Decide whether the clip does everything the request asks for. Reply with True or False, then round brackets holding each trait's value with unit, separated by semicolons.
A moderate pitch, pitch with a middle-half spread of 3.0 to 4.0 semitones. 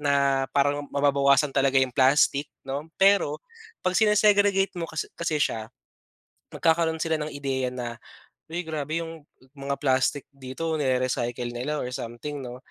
True (145 Hz; 3.5 semitones)